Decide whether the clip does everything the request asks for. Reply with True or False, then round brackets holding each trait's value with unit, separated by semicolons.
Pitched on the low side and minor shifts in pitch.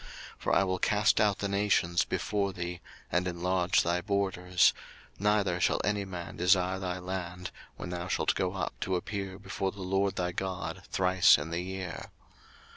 True (95 Hz; 1.7 semitones)